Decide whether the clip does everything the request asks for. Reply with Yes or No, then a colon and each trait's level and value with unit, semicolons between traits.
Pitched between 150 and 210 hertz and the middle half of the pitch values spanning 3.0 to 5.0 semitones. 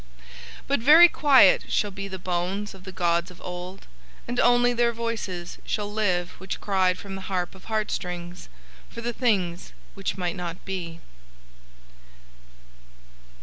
Yes: high, 190 Hz; average, 3.8 semitones